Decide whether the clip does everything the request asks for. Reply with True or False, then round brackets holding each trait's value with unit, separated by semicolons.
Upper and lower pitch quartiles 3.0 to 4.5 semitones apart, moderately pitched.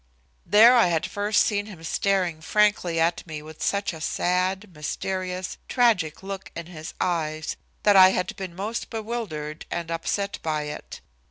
True (3.9 semitones; 180 Hz)